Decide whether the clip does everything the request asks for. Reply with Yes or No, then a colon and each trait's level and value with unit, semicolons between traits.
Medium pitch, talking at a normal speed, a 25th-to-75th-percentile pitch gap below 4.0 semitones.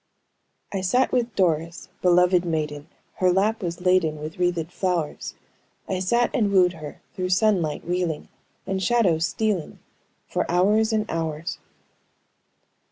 No: medium, 180 Hz; slow, 130 wpm; average, 2.9 semitones